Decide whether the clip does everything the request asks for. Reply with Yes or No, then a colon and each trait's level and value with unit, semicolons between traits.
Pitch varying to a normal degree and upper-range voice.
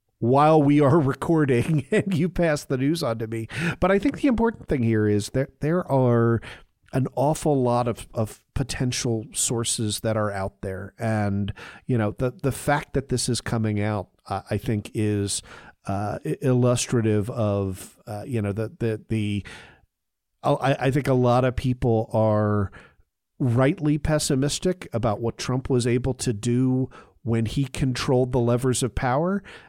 No: average, 4.2 semitones; low, 120 Hz